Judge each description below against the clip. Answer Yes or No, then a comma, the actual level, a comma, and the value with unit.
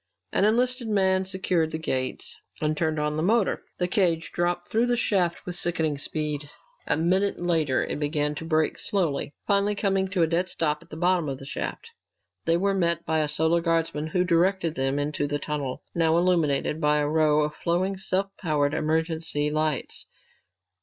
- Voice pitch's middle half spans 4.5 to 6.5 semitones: No, average, 3.6 semitones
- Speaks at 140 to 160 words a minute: No, average, 185 wpm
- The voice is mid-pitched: Yes, medium, 165 Hz